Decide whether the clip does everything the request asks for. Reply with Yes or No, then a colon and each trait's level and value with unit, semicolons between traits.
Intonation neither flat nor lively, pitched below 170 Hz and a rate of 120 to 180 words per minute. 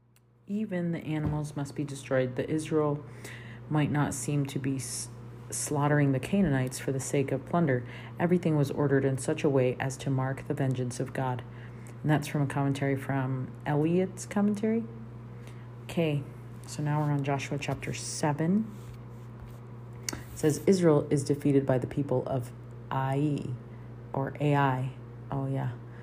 Yes: average, 3.5 semitones; low, 135 Hz; average, 150 wpm